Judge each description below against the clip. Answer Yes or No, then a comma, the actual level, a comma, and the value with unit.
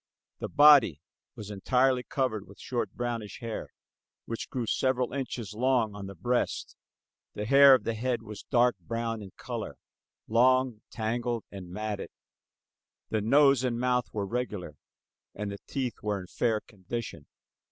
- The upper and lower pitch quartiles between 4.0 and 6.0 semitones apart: No, average, 3.2 semitones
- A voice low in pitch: Yes, low, 115 Hz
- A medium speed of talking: Yes, average, 150 wpm